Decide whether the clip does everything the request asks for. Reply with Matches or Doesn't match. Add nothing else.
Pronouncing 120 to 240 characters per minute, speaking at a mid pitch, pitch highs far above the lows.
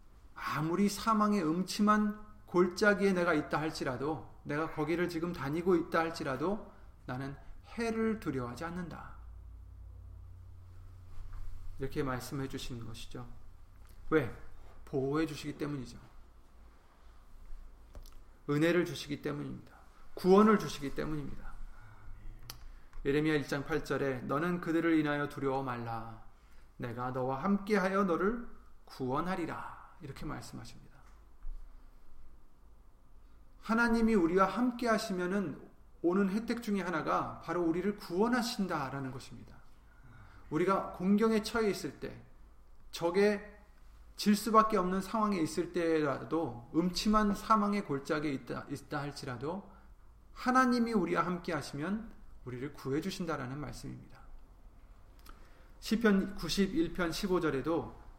Doesn't match